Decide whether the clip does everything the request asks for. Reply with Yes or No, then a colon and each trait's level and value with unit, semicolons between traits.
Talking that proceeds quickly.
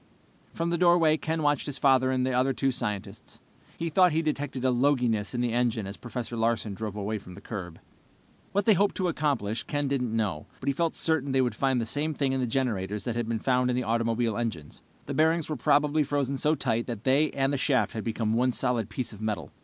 Yes: fast, 235 wpm